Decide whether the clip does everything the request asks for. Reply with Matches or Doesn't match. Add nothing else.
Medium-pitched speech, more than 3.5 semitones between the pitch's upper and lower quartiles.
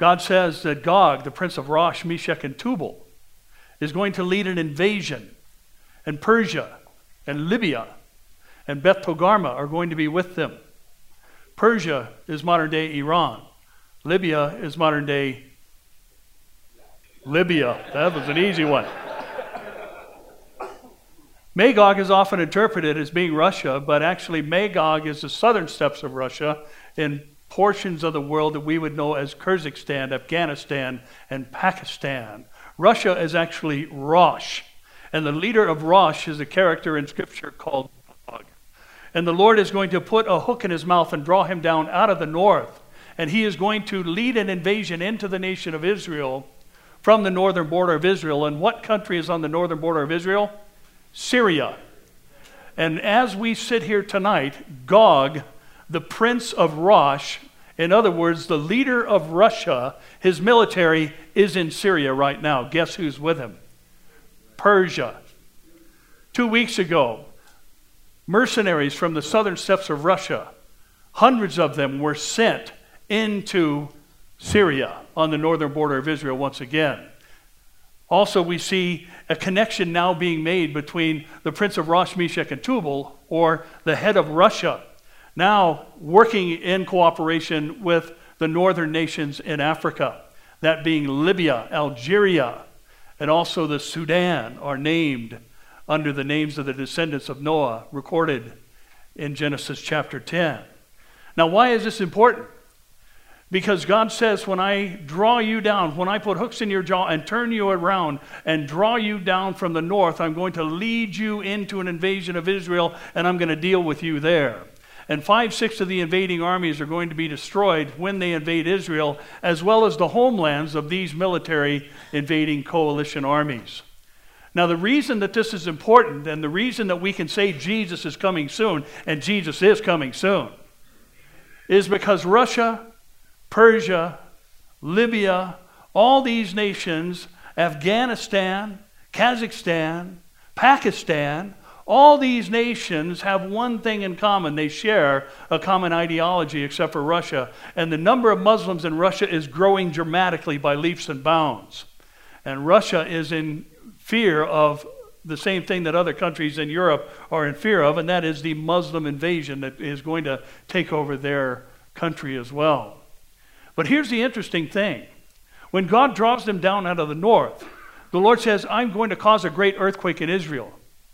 Matches